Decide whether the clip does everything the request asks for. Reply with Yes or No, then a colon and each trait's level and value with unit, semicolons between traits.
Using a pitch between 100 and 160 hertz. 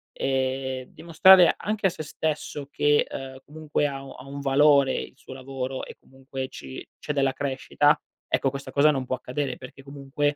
Yes: medium, 140 Hz